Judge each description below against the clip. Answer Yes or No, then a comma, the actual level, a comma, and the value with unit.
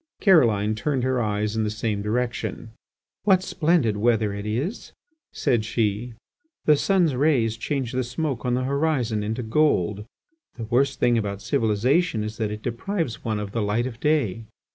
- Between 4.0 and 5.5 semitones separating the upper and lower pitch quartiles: Yes, average, 4.5 semitones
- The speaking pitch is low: Yes, low, 115 Hz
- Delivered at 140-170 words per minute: Yes, average, 165 wpm